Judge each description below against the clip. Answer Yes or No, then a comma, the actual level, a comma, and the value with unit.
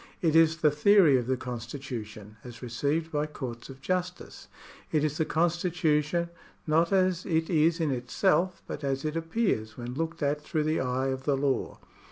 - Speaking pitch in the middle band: Yes, medium, 150 Hz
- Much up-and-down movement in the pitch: No, average, 4.0 semitones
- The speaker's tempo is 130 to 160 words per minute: No, average, 185 wpm